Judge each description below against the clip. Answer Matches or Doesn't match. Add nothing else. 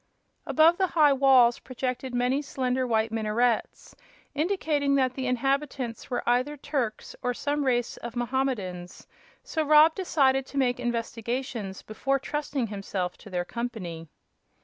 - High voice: Matches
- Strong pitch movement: Doesn't match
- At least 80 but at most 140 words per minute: Matches